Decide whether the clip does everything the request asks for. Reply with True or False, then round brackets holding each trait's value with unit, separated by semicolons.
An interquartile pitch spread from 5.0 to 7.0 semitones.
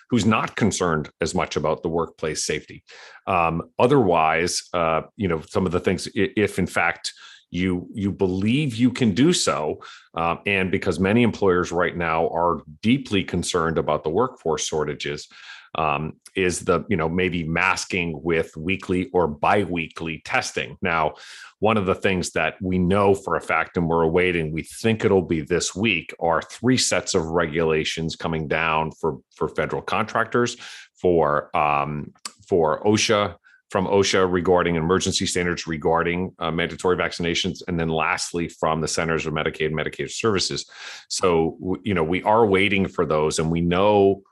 False (3.0 semitones)